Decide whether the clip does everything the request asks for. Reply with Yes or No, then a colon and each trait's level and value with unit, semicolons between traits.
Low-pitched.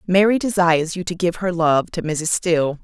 No: medium, 175 Hz